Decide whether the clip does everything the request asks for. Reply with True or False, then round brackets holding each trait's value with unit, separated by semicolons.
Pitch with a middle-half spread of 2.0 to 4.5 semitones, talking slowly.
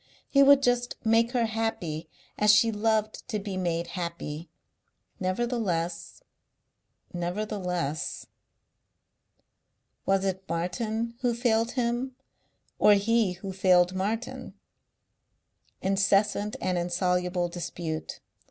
True (4.2 semitones; 95 wpm)